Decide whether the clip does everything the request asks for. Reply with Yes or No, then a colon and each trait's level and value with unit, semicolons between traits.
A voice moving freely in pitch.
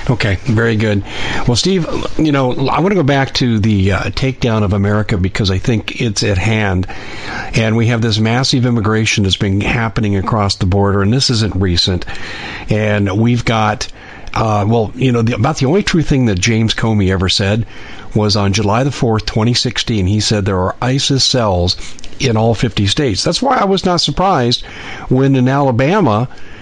No: average, 4.0 semitones